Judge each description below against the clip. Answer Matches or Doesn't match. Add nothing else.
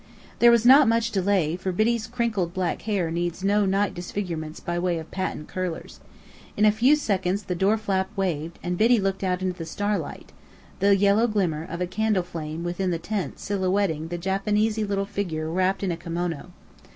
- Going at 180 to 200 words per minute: Matches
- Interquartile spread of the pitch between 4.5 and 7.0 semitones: Doesn't match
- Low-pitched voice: Doesn't match